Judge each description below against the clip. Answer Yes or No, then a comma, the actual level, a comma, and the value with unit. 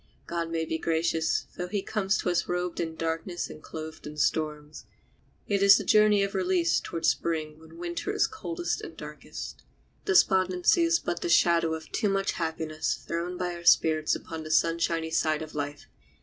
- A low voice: No, medium, 170 Hz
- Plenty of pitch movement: No, average, 2.9 semitones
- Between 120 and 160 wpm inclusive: No, average, 185 wpm